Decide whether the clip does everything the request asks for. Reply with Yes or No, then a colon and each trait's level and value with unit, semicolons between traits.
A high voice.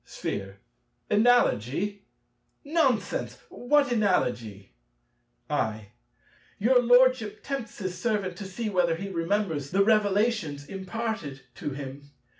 Yes: high, 200 Hz